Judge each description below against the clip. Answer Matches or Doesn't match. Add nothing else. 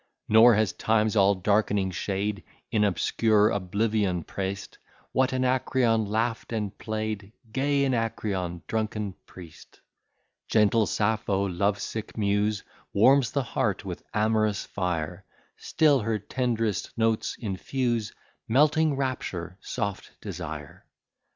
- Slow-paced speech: Matches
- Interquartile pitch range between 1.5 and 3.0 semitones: Matches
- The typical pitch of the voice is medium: Doesn't match